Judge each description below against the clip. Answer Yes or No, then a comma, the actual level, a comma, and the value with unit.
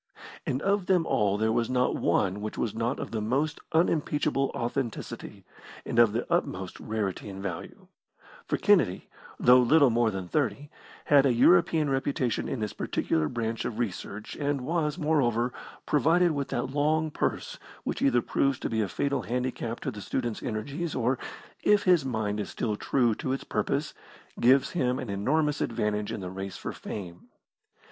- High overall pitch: No, low, 125 Hz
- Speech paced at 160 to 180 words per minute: Yes, average, 170 wpm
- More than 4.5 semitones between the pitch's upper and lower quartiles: Yes, average, 5.2 semitones